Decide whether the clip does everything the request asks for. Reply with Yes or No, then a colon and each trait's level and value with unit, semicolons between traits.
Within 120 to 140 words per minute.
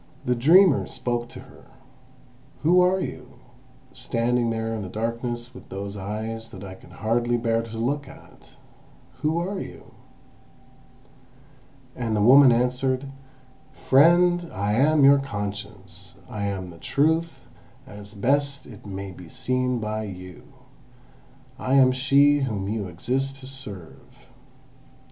Yes: slow, 135 wpm